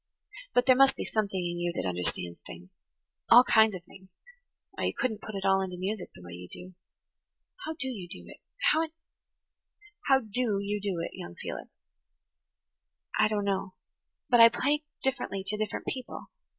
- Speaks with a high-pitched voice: Yes, high, 205 Hz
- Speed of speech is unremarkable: Yes, average, 170 wpm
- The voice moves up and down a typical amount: No, wide, 5.8 semitones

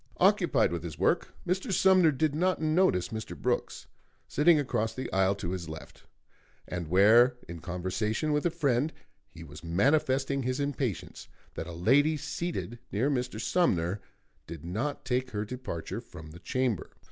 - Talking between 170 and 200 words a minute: No, average, 160 wpm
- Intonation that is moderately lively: No, wide, 8.5 semitones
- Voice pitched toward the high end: No, low, 120 Hz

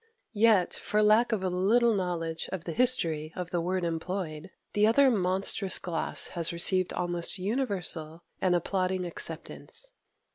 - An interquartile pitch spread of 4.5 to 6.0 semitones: No, average, 3.5 semitones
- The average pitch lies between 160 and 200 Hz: Yes, medium, 185 Hz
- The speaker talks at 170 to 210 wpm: No, average, 145 wpm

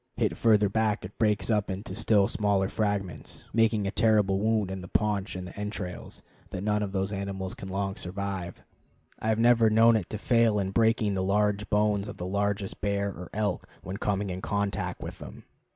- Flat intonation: Yes, narrow, 1.8 semitones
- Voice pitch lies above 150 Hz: No, low, 100 Hz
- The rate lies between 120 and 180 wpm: No, average, 195 wpm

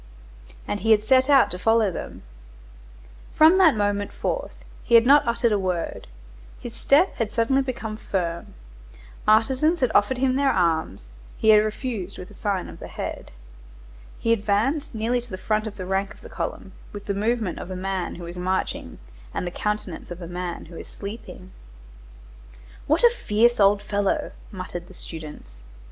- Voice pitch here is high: Yes, high, 210 Hz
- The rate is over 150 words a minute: Yes, average, 175 wpm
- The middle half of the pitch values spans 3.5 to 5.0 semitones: Yes, average, 4.5 semitones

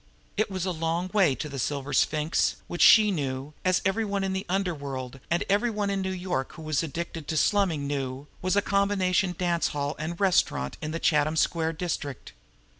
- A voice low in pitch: No, medium, 170 Hz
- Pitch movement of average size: Yes, average, 4.7 semitones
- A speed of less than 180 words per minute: No, average, 195 wpm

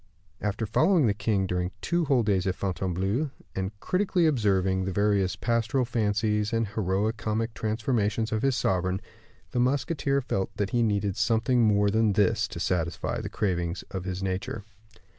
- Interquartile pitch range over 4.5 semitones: No, average, 3.5 semitones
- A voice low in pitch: Yes, low, 105 Hz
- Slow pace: No, average, 160 wpm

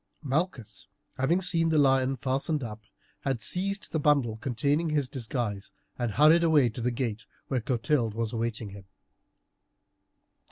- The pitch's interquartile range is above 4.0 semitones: Yes, average, 4.7 semitones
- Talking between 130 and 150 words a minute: Yes, average, 145 wpm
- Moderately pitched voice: No, low, 130 Hz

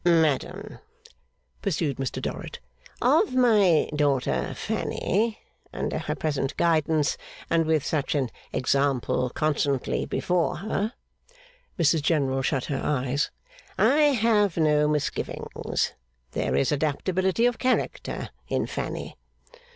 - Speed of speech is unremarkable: No, slow, 110 wpm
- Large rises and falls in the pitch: Yes, wide, 5.7 semitones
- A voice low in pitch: No, medium, 155 Hz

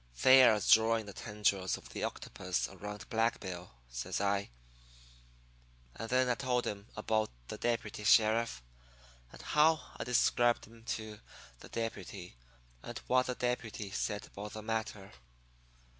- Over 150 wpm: No, average, 140 wpm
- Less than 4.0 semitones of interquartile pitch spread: Yes, average, 2.7 semitones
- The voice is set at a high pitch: No, low, 110 Hz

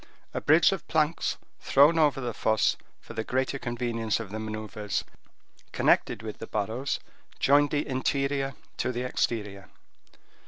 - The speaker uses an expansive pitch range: No, average, 4.4 semitones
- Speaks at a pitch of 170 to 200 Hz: No, low, 125 Hz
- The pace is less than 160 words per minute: Yes, average, 145 wpm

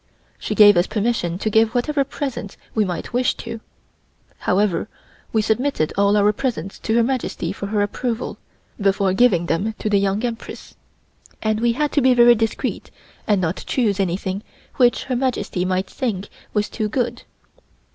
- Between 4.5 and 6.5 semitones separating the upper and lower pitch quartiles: No, average, 3.4 semitones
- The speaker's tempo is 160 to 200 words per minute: Yes, average, 165 wpm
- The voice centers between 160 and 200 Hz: No, high, 215 Hz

